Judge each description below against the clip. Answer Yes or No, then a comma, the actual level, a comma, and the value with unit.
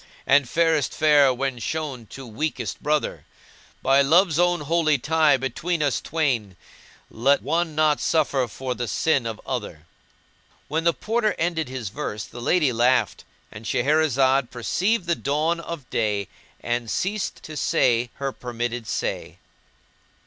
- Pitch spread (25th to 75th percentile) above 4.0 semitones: Yes, average, 4.7 semitones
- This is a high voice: No, medium, 140 Hz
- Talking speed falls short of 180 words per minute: Yes, average, 150 wpm